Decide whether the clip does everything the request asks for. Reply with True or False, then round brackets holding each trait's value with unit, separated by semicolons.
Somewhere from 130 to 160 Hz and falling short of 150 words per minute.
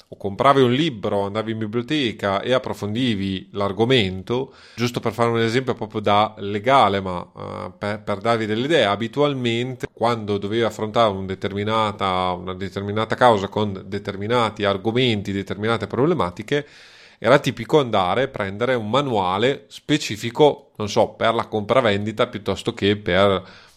False (110 Hz; 140 wpm)